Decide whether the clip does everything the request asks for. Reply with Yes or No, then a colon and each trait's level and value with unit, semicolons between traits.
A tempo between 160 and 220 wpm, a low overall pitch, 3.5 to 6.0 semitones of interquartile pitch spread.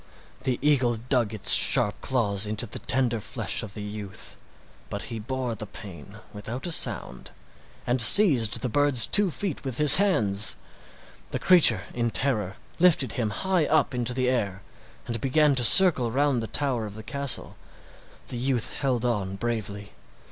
Yes: average, 165 wpm; low, 120 Hz; average, 4.5 semitones